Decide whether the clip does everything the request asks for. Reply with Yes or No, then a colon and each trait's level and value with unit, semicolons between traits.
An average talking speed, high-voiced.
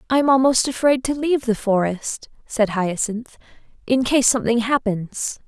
Yes: average, 145 wpm; high, 240 Hz